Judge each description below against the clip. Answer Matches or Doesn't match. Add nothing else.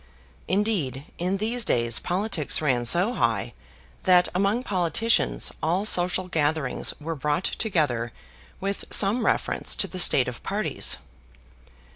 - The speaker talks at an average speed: Doesn't match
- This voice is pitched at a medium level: Matches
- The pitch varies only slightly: Doesn't match